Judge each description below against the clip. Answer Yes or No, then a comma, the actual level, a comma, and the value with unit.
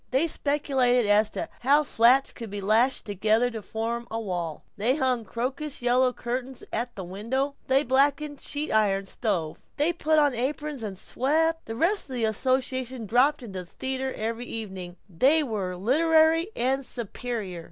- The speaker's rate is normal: Yes, average, 170 wpm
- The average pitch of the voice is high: Yes, high, 245 Hz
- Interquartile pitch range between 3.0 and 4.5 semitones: Yes, average, 4.2 semitones